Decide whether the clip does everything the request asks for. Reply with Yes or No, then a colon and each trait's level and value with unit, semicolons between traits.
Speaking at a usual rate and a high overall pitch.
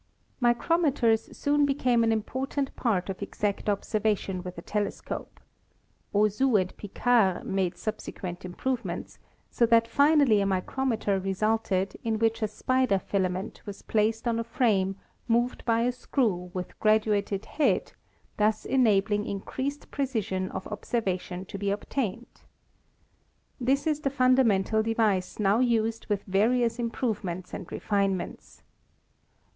No: slow, 130 wpm; high, 220 Hz